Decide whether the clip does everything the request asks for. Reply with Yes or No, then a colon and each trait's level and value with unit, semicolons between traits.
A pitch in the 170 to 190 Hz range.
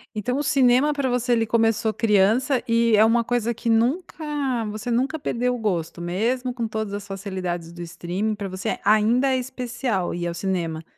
No: high, 225 Hz